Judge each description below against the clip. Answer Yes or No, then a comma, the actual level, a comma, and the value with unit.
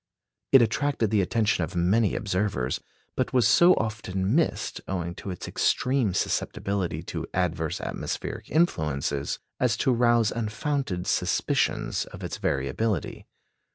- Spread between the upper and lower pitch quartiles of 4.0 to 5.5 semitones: Yes, average, 5.1 semitones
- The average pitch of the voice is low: Yes, low, 105 Hz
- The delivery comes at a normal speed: No, slow, 125 wpm